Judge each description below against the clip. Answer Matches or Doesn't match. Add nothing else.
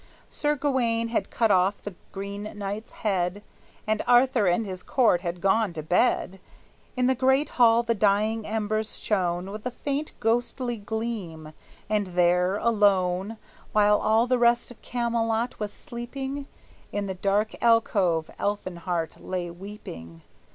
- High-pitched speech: Matches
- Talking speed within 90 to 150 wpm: Matches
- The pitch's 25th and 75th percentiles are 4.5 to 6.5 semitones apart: Doesn't match